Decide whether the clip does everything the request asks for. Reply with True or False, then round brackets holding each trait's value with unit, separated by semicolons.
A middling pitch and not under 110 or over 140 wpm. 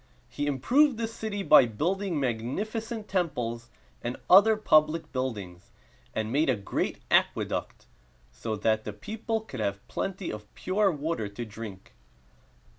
True (145 Hz; 135 wpm)